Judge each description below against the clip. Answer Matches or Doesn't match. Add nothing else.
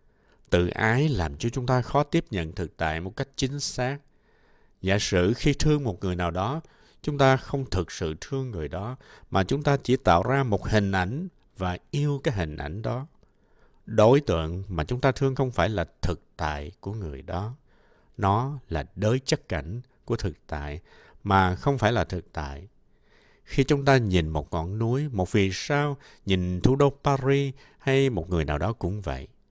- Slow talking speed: Doesn't match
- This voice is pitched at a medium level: Doesn't match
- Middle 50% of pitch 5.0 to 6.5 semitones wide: Doesn't match